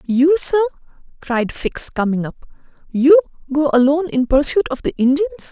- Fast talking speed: No, average, 150 wpm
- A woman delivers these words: Yes, female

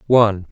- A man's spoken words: Yes, male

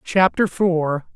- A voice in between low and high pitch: Yes, medium, 175 Hz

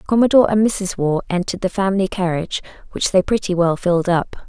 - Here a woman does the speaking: Yes, female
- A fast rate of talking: No, average, 190 wpm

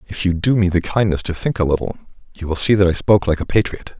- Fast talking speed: Yes, fast, 285 wpm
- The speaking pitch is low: Yes, very low, 90 Hz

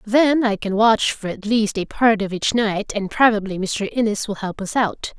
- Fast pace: Yes, fast, 230 wpm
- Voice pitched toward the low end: No, high, 215 Hz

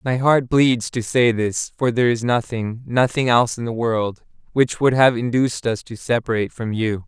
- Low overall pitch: Yes, low, 120 Hz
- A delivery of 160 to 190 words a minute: Yes, average, 185 wpm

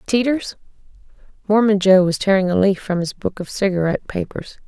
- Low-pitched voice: No, high, 195 Hz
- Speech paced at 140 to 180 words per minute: Yes, average, 165 wpm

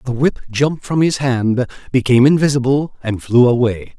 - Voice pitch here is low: Yes, low, 130 Hz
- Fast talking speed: No, average, 165 wpm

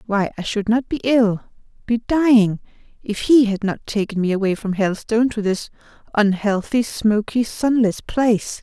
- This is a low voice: No, high, 220 Hz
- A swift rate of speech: No, average, 145 wpm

